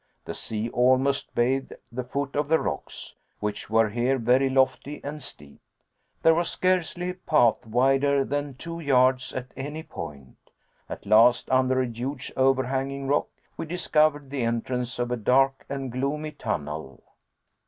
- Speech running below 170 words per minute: Yes, average, 155 wpm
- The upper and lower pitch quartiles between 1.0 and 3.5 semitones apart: Yes, average, 2.9 semitones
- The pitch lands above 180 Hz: No, low, 130 Hz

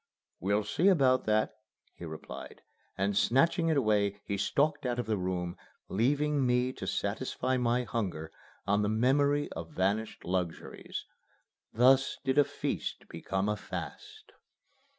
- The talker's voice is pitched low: Yes, low, 115 Hz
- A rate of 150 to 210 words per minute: No, average, 140 wpm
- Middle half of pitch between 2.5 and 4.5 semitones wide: No, average, 5.2 semitones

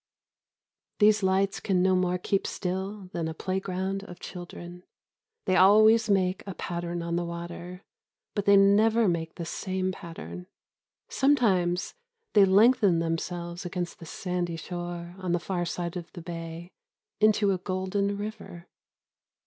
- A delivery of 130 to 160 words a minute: Yes, average, 140 wpm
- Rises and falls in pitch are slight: Yes, narrow, 2.2 semitones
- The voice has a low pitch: No, medium, 185 Hz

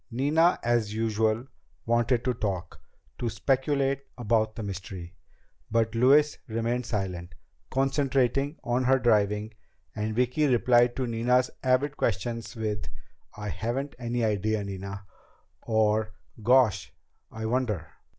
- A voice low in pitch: Yes, low, 115 Hz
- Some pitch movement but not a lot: Yes, average, 3.2 semitones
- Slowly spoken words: Yes, slow, 120 wpm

